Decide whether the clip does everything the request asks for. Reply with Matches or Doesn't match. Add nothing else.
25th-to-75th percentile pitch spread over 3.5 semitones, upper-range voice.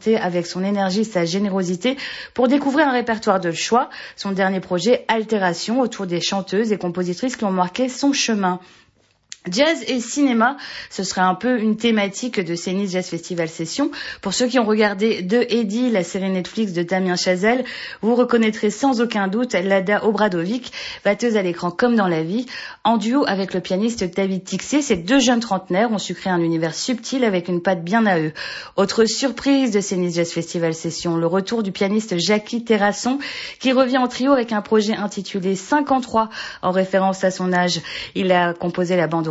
Matches